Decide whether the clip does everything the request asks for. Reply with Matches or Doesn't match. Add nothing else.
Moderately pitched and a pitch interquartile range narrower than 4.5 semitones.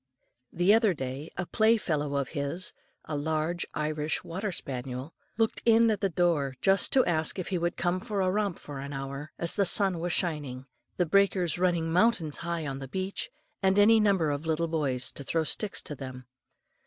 Doesn't match